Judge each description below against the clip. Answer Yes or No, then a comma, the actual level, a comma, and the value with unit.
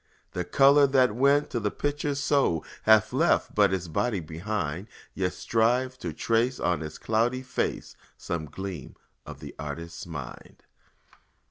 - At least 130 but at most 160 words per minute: Yes, average, 145 wpm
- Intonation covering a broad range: Yes, wide, 7.1 semitones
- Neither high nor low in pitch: No, low, 105 Hz